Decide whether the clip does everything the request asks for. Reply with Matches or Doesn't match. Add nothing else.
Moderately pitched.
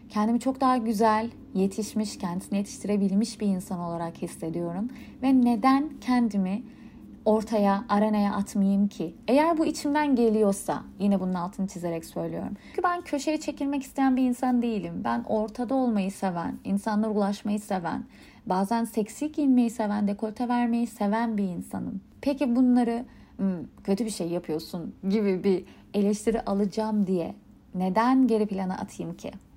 Doesn't match